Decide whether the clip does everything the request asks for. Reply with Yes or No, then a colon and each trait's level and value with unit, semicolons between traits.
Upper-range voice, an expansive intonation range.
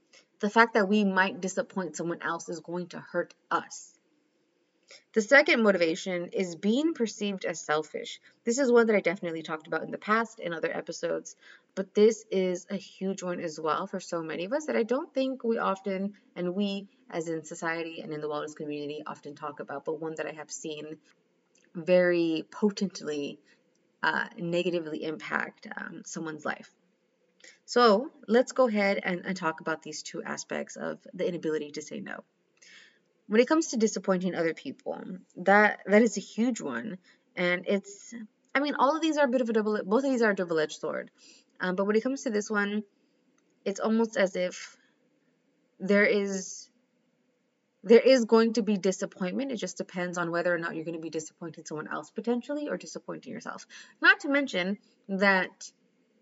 Yes: high, 195 Hz; wide, 5.7 semitones